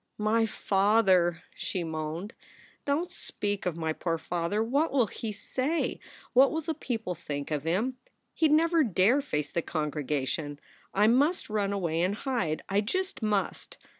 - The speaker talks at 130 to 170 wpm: Yes, average, 165 wpm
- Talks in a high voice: Yes, high, 205 Hz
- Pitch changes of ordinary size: No, wide, 7.5 semitones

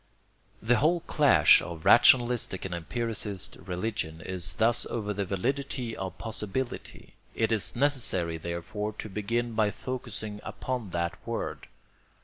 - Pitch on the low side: Yes, low, 105 Hz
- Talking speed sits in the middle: No, slow, 130 wpm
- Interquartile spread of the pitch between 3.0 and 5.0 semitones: Yes, average, 4.4 semitones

